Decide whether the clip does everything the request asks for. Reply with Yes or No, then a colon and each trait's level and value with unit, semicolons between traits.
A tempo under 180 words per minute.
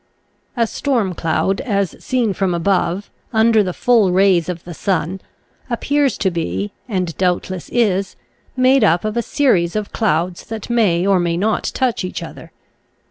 Yes: average, 160 wpm